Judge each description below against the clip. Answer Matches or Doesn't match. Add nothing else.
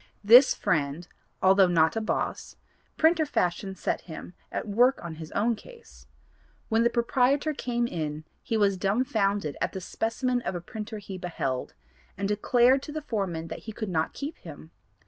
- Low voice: Doesn't match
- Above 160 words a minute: Matches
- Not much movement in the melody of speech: Doesn't match